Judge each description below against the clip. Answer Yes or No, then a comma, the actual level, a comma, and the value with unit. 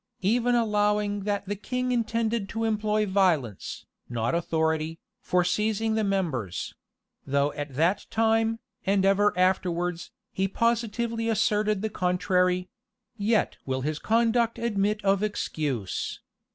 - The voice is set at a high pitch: Yes, high, 200 Hz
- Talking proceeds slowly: Yes, slow, 125 wpm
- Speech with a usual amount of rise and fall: Yes, average, 3.9 semitones